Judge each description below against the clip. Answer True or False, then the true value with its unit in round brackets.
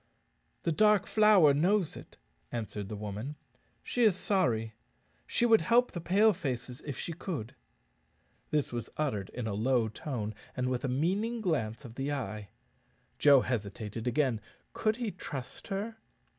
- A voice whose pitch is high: False (140 Hz)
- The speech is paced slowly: False (155 wpm)